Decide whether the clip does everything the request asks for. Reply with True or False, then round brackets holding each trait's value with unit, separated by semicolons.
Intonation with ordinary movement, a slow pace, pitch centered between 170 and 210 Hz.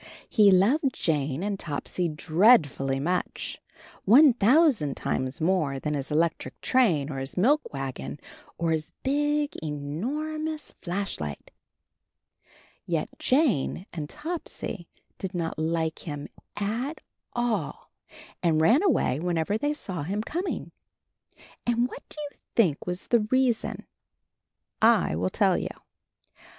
False (8.7 semitones; 130 wpm; 185 Hz)